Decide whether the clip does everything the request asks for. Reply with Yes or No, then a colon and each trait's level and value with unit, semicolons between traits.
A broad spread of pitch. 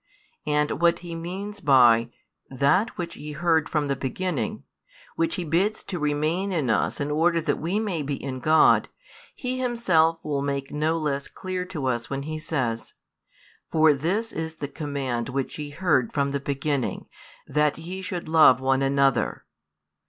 No: average, 3.9 semitones